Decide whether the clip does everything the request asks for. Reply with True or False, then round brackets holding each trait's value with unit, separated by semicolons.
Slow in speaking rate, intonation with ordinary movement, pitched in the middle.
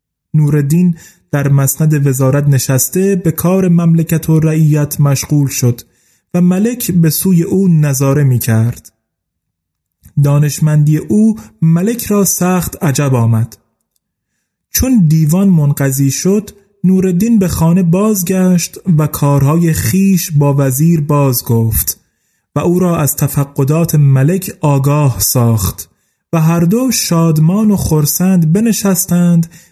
False (115 wpm; 4.5 semitones; 155 Hz)